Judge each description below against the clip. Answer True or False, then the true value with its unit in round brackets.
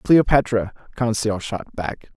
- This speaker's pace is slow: True (110 wpm)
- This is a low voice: True (110 Hz)